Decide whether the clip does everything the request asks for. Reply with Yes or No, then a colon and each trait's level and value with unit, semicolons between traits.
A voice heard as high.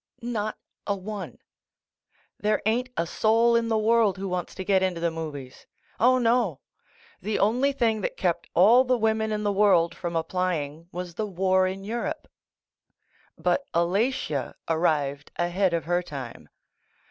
Yes: high, 195 Hz